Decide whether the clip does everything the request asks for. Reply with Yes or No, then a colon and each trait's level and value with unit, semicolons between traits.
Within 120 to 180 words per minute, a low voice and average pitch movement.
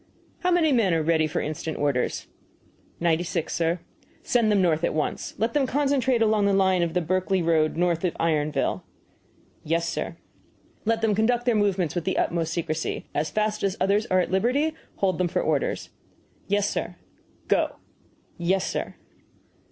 No: average, 170 wpm; medium, 185 Hz; average, 4.8 semitones